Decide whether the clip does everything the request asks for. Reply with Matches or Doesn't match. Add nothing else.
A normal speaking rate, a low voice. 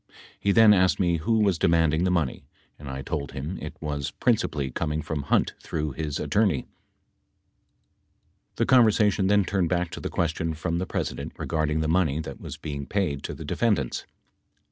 Matches